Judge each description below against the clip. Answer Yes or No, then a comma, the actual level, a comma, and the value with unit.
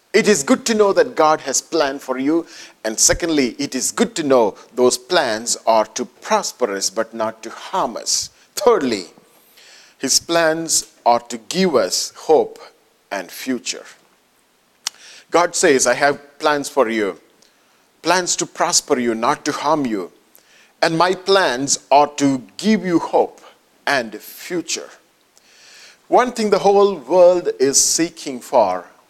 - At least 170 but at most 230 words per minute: No, average, 150 wpm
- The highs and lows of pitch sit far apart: Yes, wide, 5.9 semitones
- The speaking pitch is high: No, medium, 150 Hz